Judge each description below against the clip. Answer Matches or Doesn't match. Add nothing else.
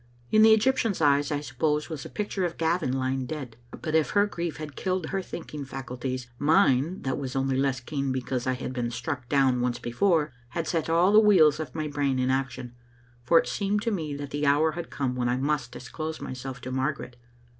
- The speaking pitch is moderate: Matches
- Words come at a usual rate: Doesn't match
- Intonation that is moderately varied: Matches